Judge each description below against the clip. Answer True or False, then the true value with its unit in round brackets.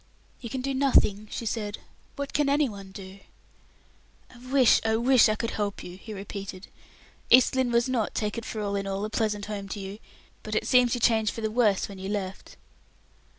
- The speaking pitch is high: True (215 Hz)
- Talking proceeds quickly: True (210 wpm)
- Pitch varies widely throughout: False (3.4 semitones)